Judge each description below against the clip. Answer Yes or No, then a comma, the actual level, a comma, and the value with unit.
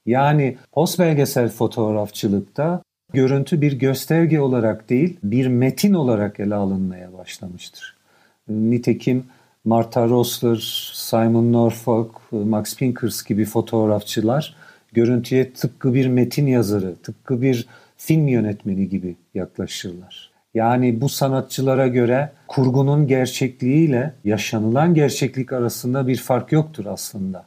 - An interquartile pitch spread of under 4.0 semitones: Yes, average, 3.6 semitones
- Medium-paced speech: Yes, average, 105 wpm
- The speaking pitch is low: Yes, low, 125 Hz